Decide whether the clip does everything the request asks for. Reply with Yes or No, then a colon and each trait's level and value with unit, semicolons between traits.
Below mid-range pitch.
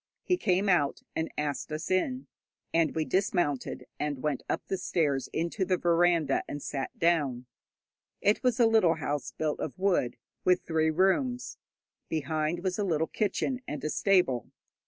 No: medium, 165 Hz